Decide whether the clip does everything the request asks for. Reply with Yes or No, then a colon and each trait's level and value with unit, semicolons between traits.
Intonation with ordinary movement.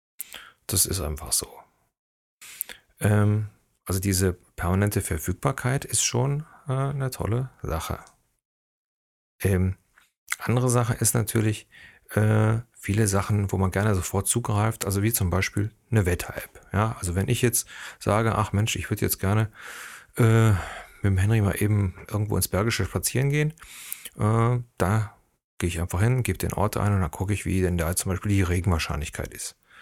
Yes: average, 3.1 semitones